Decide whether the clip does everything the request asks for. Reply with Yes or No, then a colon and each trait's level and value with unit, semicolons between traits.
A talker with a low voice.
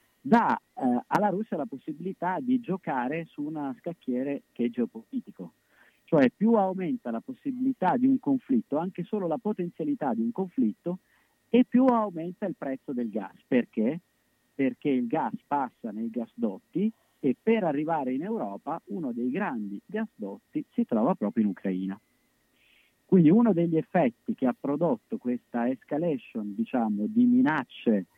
No: high, 210 Hz